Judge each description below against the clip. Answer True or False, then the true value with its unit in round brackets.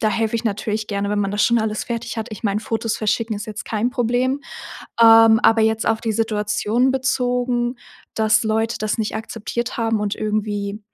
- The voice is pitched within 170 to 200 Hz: False (220 Hz)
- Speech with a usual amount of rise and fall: False (1.7 semitones)